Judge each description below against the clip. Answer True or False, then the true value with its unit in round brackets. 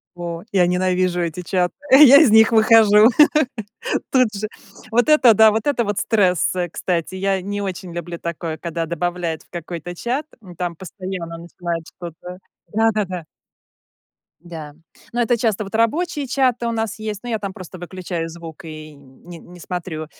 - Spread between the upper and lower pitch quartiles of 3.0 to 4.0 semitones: False (4.4 semitones)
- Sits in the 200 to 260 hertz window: False (185 Hz)